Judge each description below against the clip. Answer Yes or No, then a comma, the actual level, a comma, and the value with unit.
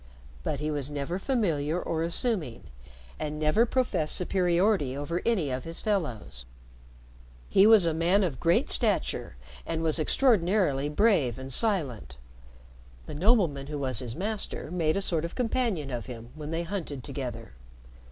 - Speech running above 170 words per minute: No, average, 150 wpm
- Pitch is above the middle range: No, medium, 160 Hz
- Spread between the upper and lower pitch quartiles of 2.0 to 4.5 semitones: No, wide, 5.6 semitones